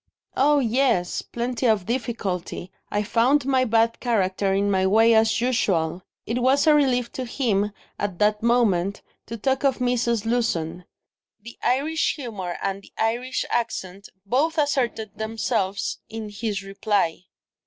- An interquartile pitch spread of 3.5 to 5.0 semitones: Yes, average, 3.9 semitones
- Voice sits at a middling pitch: No, high, 225 Hz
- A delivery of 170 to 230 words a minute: No, average, 145 wpm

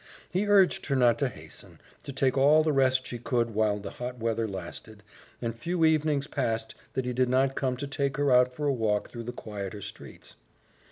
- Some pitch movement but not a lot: Yes, average, 3.6 semitones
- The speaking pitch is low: Yes, low, 125 Hz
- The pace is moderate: No, fast, 210 wpm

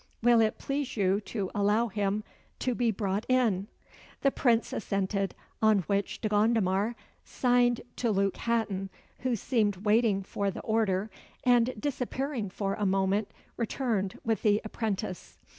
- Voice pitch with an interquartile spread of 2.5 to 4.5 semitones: Yes, average, 3.1 semitones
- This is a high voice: Yes, high, 215 Hz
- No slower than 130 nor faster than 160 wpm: Yes, average, 140 wpm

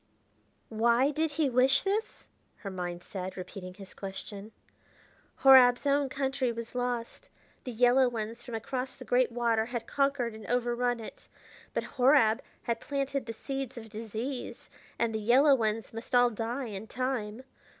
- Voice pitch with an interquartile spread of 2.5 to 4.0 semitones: Yes, average, 3.1 semitones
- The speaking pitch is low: No, high, 240 Hz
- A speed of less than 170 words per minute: Yes, average, 155 wpm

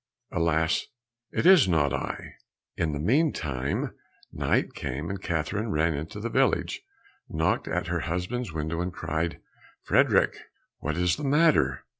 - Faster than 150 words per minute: No, average, 140 wpm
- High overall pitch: No, very low, 85 Hz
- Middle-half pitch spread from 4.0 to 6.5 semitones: Yes, average, 4.6 semitones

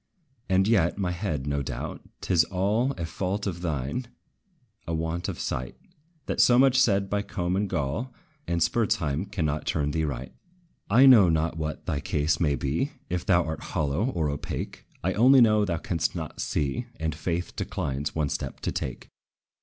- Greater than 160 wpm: Yes, average, 180 wpm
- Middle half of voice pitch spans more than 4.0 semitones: Yes, average, 5.0 semitones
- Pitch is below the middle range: Yes, very low, 85 Hz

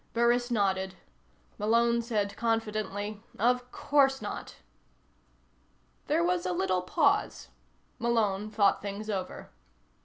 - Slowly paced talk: Yes, slow, 100 wpm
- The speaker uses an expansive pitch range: No, average, 3.3 semitones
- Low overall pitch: No, high, 215 Hz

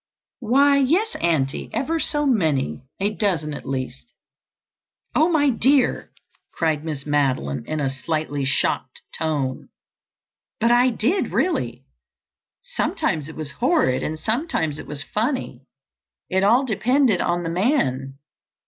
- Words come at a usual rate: No, slow, 130 wpm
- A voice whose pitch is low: No, medium, 170 Hz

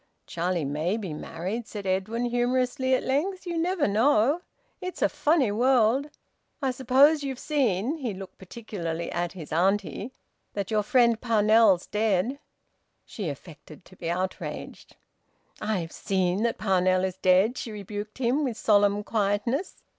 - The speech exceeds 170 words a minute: No, average, 145 wpm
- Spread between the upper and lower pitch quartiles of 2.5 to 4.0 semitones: No, wide, 5.4 semitones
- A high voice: Yes, high, 215 Hz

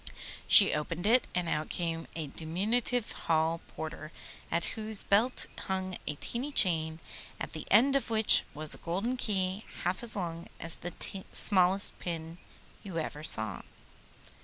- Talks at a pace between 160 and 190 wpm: No, average, 150 wpm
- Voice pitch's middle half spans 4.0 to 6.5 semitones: Yes, average, 4.6 semitones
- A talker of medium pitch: Yes, medium, 180 Hz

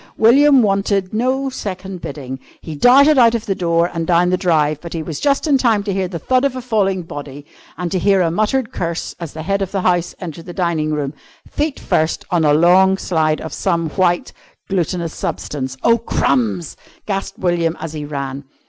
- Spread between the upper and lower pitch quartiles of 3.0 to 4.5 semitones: Yes, average, 4.2 semitones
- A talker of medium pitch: Yes, medium, 180 Hz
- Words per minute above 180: Yes, average, 200 wpm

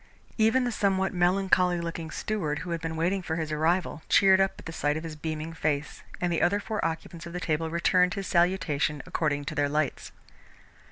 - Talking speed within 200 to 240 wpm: Yes, fast, 205 wpm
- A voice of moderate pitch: Yes, medium, 170 Hz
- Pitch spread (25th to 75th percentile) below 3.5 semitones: Yes, average, 3.1 semitones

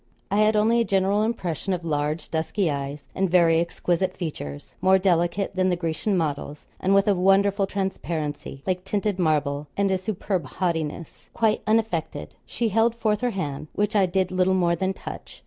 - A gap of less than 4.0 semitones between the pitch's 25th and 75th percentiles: Yes, average, 3.6 semitones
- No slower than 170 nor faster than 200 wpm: Yes, average, 180 wpm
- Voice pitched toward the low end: No, medium, 185 Hz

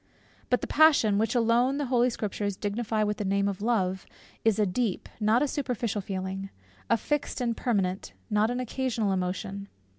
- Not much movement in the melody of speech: No, average, 3.6 semitones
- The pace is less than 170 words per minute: No, average, 175 wpm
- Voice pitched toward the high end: Yes, high, 215 Hz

